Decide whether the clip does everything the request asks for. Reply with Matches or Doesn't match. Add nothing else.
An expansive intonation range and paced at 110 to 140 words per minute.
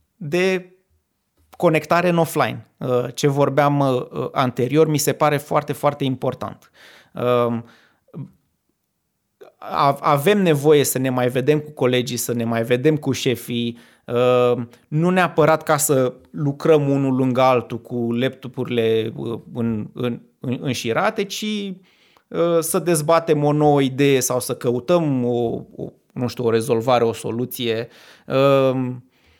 Doesn't match